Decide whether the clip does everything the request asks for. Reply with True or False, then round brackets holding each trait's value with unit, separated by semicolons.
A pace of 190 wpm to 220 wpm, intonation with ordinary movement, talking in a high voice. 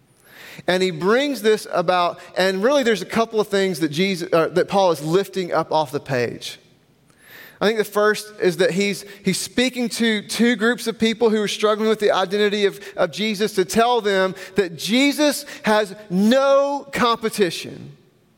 False (175 wpm; 3.4 semitones; 200 Hz)